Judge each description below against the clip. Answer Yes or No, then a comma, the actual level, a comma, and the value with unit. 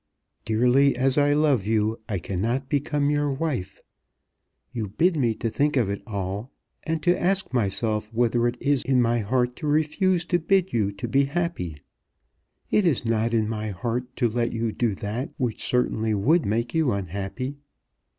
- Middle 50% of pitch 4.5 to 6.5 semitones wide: Yes, average, 5.0 semitones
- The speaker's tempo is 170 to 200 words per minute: Yes, average, 175 wpm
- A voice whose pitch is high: No, low, 120 Hz